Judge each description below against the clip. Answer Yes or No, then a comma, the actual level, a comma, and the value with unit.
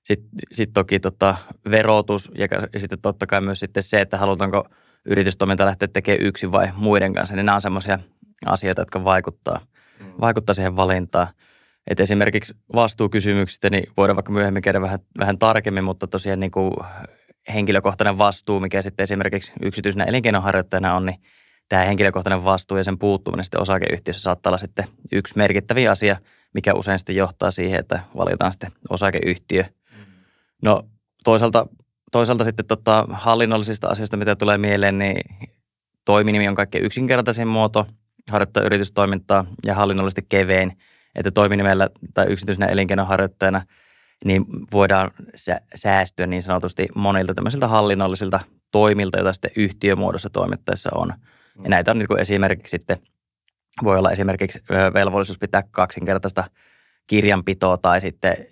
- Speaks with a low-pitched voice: Yes, low, 100 Hz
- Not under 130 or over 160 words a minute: Yes, average, 135 wpm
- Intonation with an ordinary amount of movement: No, narrow, 1.3 semitones